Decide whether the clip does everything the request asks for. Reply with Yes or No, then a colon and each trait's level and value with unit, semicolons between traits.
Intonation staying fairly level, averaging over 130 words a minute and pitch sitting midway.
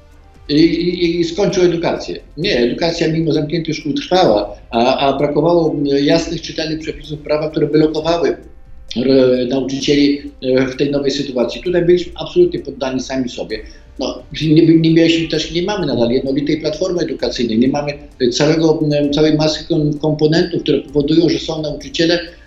No: average, 3.2 semitones; average, 145 wpm; medium, 150 Hz